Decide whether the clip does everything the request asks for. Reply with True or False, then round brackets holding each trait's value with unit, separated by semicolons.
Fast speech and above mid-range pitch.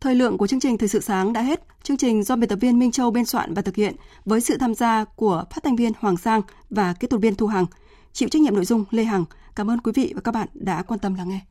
True (305 wpm; 225 Hz)